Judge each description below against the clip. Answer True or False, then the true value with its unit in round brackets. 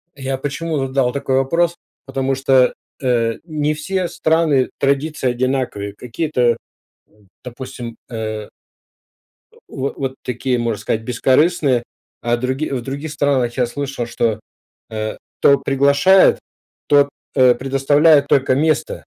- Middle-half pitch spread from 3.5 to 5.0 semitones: False (2.7 semitones)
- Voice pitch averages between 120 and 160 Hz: True (135 Hz)